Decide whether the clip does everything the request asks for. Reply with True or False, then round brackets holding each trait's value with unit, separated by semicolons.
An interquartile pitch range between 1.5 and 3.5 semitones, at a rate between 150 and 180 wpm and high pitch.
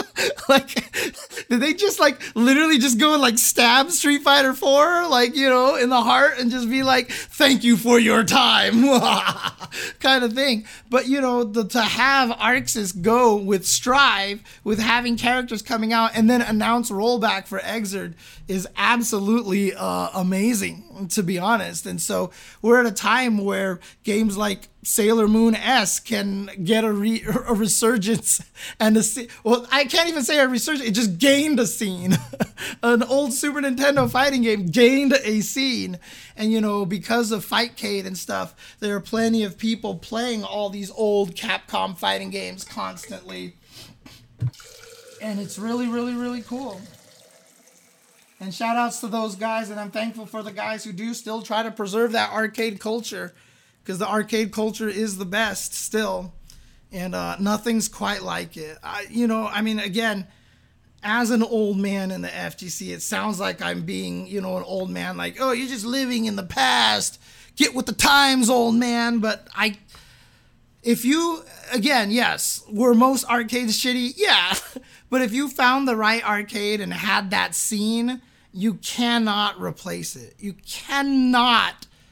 True (3.2 semitones; 165 wpm; 225 Hz)